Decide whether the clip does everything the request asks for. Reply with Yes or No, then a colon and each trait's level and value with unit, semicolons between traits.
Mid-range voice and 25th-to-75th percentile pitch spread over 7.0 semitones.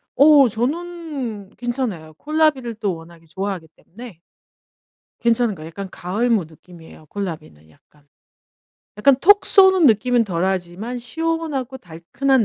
No: high, 225 Hz; wide, 7.6 semitones